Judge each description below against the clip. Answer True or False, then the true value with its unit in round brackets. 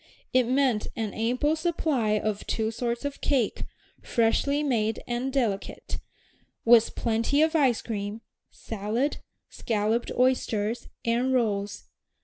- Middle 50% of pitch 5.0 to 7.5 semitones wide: False (3.3 semitones)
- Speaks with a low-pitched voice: False (235 Hz)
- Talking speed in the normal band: False (120 wpm)